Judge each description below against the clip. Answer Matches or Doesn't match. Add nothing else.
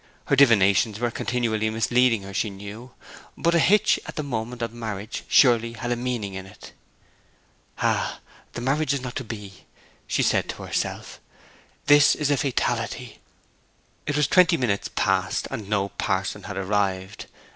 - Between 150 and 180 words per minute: Matches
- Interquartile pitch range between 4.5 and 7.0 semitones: Doesn't match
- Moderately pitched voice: Doesn't match